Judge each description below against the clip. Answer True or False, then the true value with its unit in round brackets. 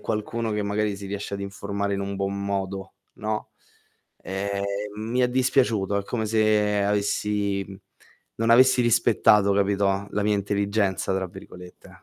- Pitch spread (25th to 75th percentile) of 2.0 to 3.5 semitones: False (1.5 semitones)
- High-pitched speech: False (100 Hz)